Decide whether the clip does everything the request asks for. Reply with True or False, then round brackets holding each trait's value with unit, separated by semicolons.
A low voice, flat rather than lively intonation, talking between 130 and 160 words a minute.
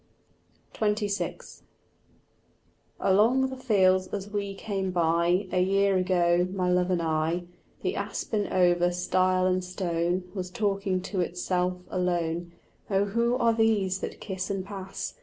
False (185 Hz; 2.0 semitones; 135 wpm)